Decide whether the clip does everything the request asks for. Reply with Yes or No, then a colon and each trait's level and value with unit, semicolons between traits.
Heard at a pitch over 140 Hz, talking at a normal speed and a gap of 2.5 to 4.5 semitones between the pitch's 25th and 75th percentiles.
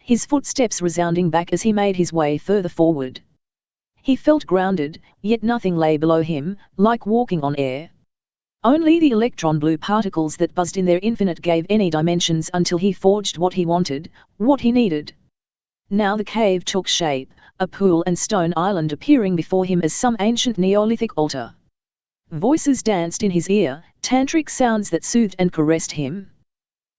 No: medium, 185 Hz; average, 165 wpm; average, 4.9 semitones